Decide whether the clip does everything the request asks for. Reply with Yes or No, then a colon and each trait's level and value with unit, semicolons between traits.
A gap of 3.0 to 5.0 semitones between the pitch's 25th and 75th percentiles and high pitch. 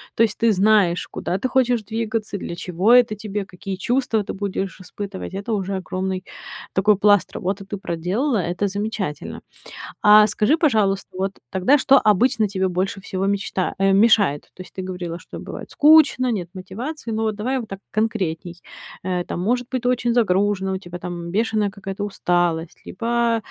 Yes: average, 3.3 semitones; high, 200 Hz